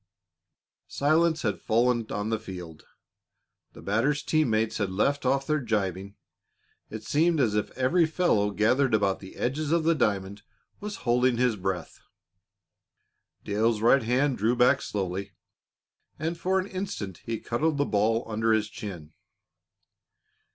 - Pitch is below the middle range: Yes, low, 115 Hz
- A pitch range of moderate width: No, wide, 5.9 semitones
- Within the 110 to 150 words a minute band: Yes, average, 145 wpm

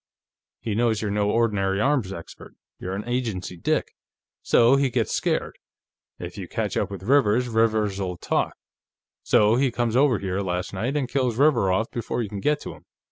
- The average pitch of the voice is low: Yes, low, 110 Hz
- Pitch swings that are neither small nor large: Yes, average, 4.0 semitones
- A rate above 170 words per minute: Yes, average, 185 wpm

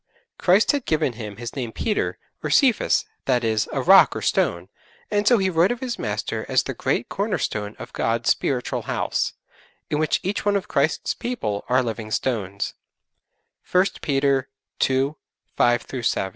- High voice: No, low, 135 Hz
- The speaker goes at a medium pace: Yes, average, 170 wpm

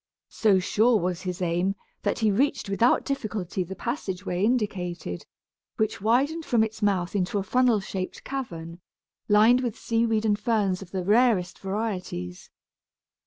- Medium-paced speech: Yes, average, 150 wpm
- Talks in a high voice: Yes, high, 205 Hz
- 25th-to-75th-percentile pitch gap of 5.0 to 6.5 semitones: No, average, 3.9 semitones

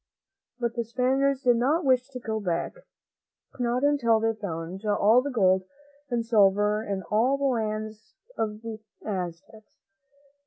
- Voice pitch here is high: Yes, high, 225 Hz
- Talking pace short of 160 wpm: Yes, average, 150 wpm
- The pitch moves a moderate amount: Yes, average, 3.3 semitones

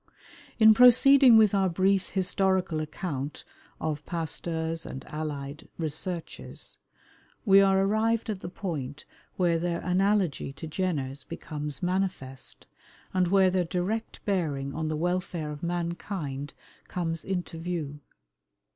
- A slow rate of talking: Yes, slow, 120 wpm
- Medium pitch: Yes, medium, 175 Hz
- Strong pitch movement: No, average, 3.8 semitones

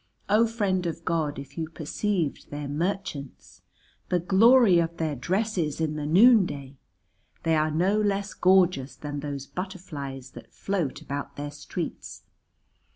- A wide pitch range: No, average, 4.8 semitones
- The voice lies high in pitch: No, medium, 165 Hz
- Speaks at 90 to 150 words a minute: Yes, average, 140 wpm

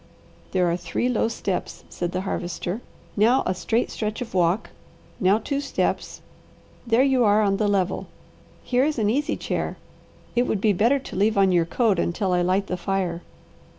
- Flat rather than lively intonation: No, average, 4.1 semitones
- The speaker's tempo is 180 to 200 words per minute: Yes, average, 185 wpm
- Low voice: No, high, 205 Hz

